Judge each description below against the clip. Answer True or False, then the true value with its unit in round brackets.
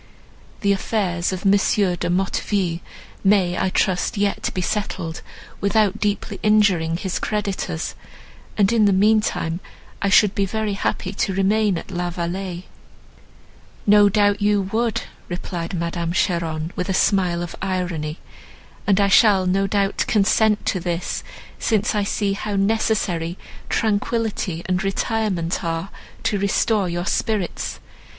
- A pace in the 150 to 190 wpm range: False (135 wpm)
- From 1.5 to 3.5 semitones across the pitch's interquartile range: True (2.8 semitones)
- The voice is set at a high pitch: True (195 Hz)